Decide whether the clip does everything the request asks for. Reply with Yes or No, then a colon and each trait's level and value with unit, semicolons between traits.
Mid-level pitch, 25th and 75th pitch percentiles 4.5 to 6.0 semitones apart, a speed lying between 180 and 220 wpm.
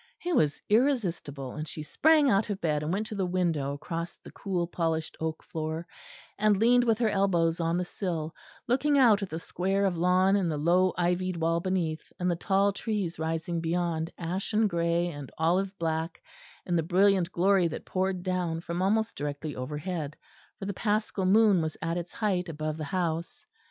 No: medium, 175 Hz; average, 3.2 semitones; average, 185 wpm